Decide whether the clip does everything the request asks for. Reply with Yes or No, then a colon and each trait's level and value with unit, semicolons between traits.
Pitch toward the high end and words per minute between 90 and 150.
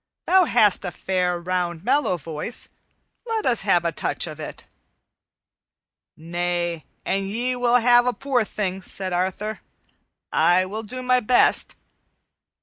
Yes: high, 195 Hz; average, 140 wpm